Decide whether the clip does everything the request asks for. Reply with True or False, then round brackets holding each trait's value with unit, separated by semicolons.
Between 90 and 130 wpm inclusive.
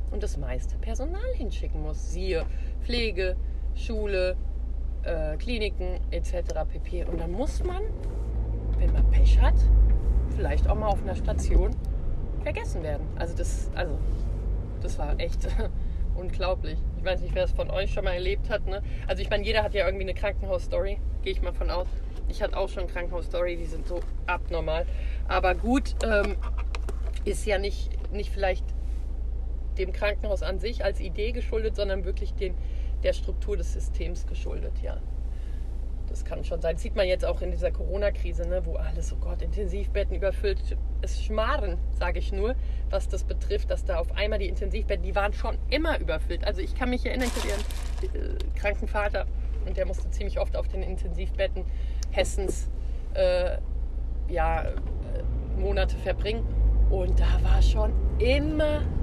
False (165 wpm)